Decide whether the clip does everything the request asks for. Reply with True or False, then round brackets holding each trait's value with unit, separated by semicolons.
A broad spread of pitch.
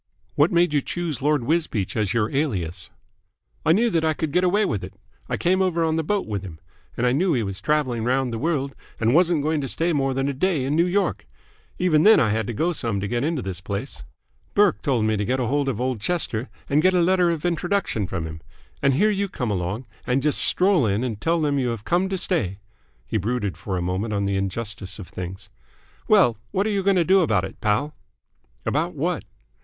True (8.1 semitones)